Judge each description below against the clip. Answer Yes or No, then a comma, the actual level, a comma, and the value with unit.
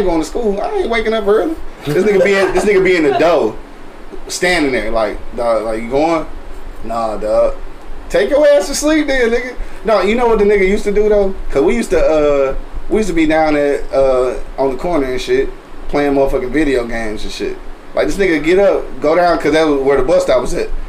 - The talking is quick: Yes, fast, 240 wpm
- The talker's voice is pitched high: Yes, high, 195 Hz